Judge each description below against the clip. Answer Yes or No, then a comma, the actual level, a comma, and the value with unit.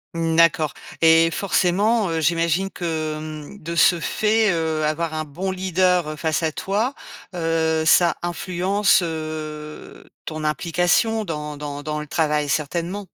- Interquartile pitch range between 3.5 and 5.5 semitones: No, average, 2.9 semitones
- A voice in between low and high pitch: Yes, medium, 165 Hz